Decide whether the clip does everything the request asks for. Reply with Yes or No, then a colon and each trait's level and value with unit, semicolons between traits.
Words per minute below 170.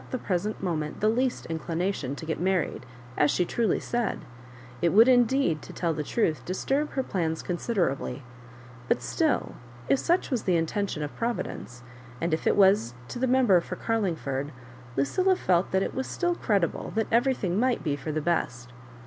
No: average, 180 wpm